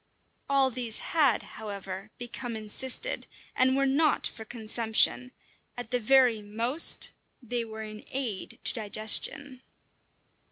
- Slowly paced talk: Yes, slow, 120 wpm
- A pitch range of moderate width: Yes, average, 3.3 semitones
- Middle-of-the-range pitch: No, high, 240 Hz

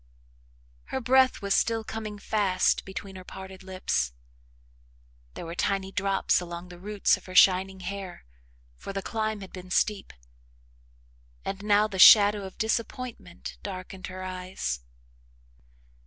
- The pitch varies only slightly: Yes, narrow, 2.2 semitones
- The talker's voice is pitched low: No, high, 195 Hz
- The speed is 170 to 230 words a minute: No, slow, 135 wpm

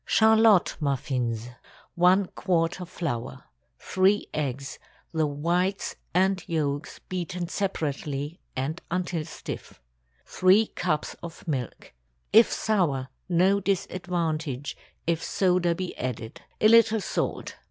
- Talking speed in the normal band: No, slow, 110 wpm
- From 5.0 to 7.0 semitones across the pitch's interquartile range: No, average, 4.5 semitones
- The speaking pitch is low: No, medium, 170 Hz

